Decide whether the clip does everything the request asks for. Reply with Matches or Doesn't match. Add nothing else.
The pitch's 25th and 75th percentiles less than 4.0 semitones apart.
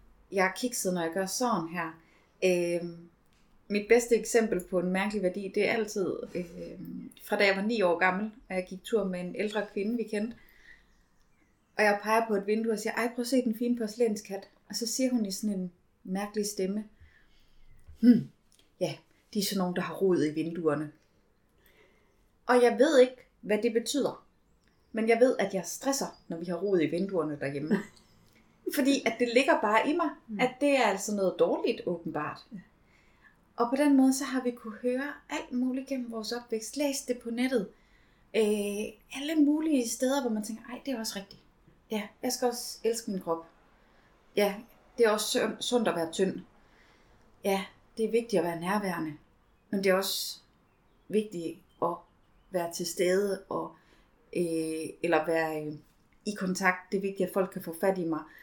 Doesn't match